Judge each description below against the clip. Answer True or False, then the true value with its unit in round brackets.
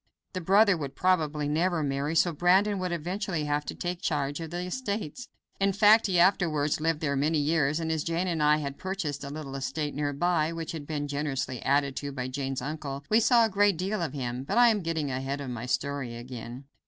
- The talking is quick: True (220 wpm)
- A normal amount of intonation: True (4.2 semitones)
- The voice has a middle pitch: True (155 Hz)